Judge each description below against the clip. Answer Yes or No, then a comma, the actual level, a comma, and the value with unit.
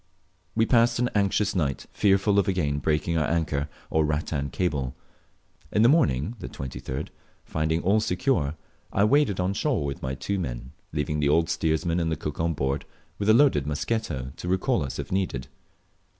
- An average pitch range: No, wide, 5.7 semitones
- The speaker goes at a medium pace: Yes, average, 170 wpm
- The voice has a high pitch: No, very low, 80 Hz